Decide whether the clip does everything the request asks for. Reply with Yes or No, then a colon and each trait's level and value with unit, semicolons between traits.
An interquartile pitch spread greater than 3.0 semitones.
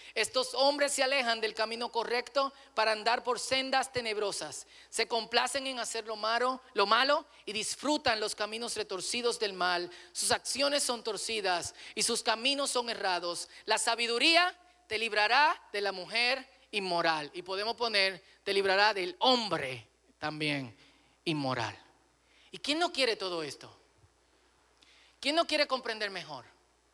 Yes: average, 4.9 semitones